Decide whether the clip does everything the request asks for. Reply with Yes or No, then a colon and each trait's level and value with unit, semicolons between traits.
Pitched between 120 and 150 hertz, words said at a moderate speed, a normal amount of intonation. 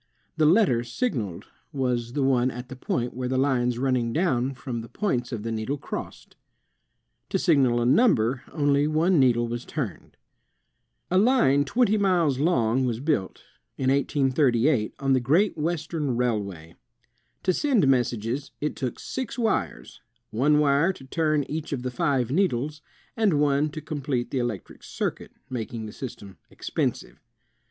Yes: low, 135 Hz; average, 150 wpm; average, 4.2 semitones